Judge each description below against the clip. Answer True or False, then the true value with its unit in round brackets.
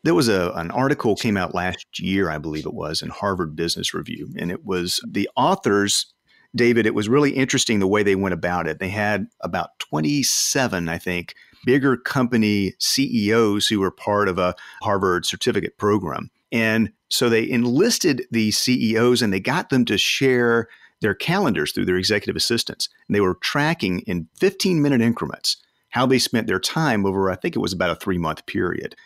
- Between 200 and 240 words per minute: False (190 wpm)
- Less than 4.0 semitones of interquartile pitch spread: False (4.7 semitones)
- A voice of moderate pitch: False (110 Hz)